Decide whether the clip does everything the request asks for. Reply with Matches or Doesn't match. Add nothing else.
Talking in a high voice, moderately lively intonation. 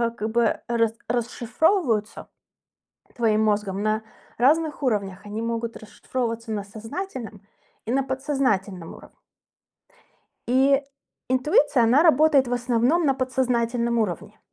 Matches